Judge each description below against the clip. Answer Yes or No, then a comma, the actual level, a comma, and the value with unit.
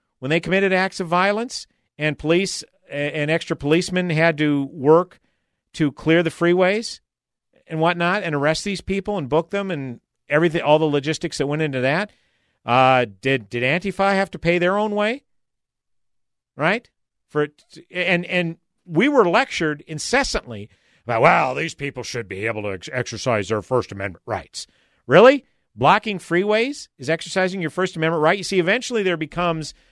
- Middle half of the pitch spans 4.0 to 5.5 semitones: Yes, average, 4.4 semitones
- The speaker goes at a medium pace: Yes, average, 165 wpm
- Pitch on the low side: No, medium, 165 Hz